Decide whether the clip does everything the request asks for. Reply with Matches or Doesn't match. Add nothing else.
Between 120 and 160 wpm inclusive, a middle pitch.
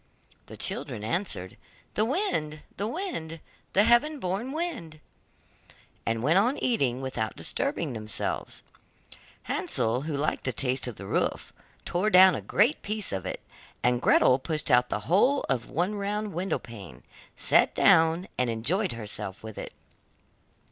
Matches